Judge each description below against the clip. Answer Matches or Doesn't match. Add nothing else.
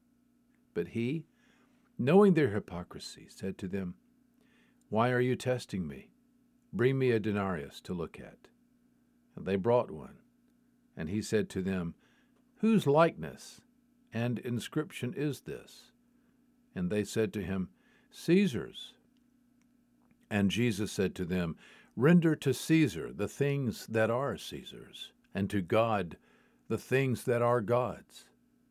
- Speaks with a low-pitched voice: Doesn't match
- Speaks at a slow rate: Matches